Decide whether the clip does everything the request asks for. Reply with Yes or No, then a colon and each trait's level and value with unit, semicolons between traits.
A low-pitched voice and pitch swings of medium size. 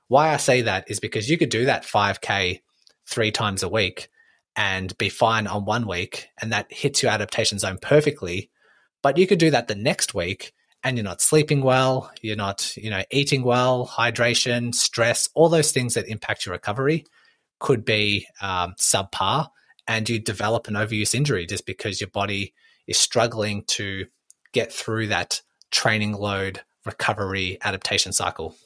Yes: low, 110 Hz; average, 3.9 semitones